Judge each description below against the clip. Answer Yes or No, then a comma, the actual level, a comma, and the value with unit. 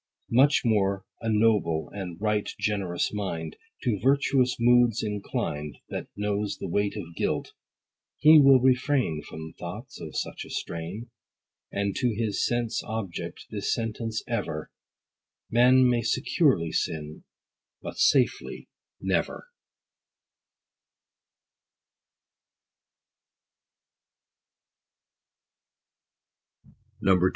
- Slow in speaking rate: Yes, slow, 90 wpm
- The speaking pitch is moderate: No, low, 105 Hz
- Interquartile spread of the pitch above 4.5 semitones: No, average, 4.2 semitones